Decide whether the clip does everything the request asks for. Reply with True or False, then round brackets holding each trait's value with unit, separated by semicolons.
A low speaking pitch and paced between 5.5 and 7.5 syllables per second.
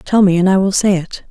False (190 Hz; 5.6 syllables/s)